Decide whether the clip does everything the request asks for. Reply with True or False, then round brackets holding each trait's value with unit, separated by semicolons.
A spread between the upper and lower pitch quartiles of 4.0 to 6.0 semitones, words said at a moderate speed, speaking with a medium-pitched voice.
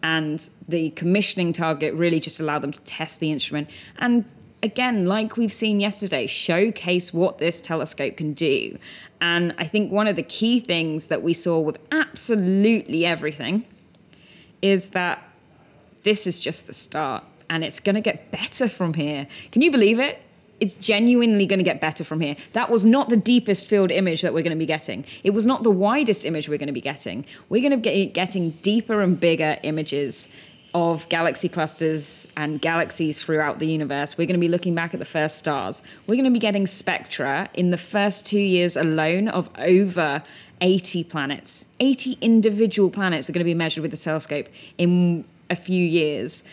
True (4.5 semitones; 190 wpm; 175 Hz)